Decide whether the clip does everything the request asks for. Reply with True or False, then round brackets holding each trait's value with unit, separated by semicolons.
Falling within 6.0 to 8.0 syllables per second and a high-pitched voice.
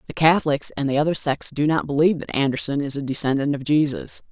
False (6.5 syllables/s; 145 Hz)